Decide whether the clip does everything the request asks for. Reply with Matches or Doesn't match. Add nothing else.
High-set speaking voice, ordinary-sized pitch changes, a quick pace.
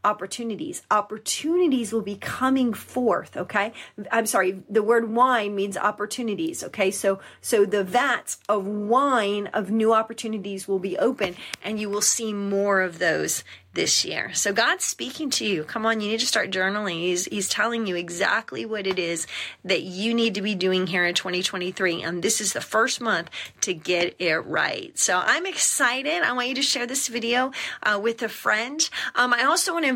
Doesn't match